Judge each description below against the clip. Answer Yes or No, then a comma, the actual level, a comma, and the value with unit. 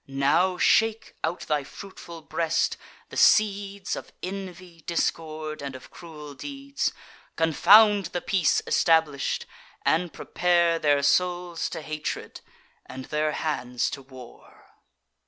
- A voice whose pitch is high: No, medium, 165 Hz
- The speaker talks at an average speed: No, slow, 120 wpm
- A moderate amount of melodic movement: Yes, average, 3.5 semitones